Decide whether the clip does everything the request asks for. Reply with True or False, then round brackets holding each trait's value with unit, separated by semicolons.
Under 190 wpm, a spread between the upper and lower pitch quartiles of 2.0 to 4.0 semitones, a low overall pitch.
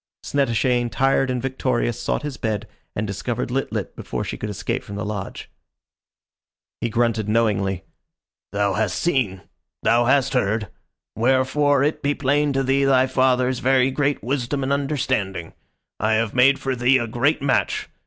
True (160 wpm; 3.7 semitones; 125 Hz)